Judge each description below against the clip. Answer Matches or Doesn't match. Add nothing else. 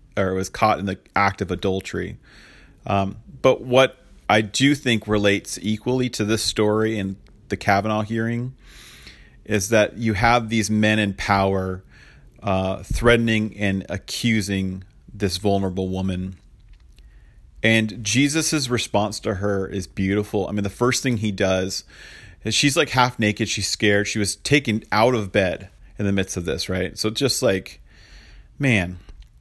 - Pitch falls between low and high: Doesn't match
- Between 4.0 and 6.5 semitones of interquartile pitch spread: Doesn't match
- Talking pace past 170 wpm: Doesn't match